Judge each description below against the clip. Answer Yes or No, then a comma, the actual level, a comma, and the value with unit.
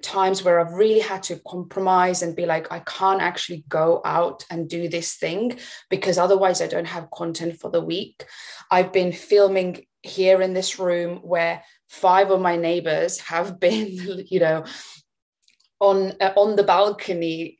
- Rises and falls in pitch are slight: Yes, narrow, 2.1 semitones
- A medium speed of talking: Yes, average, 165 wpm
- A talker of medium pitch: Yes, medium, 180 Hz